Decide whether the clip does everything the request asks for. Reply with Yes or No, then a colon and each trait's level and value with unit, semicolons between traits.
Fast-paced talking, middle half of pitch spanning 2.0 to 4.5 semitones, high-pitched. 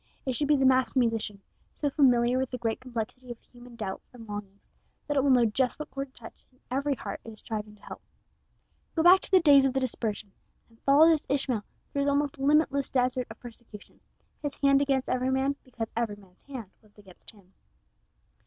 Yes: fast, 210 wpm; average, 3.6 semitones; very high, 255 Hz